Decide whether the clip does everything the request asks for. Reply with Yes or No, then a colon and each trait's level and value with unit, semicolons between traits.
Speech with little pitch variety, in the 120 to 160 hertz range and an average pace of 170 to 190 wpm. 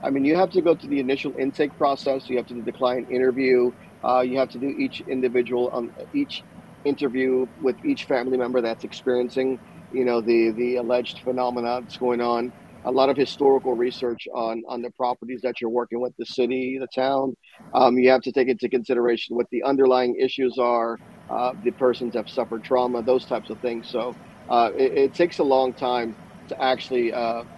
No: narrow, 1.4 semitones; low, 125 Hz; fast, 205 wpm